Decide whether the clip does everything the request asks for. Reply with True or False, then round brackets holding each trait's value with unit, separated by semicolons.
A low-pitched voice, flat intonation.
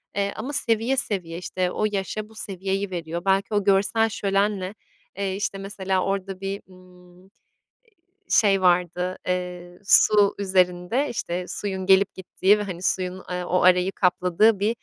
False (190 Hz; 1.9 semitones)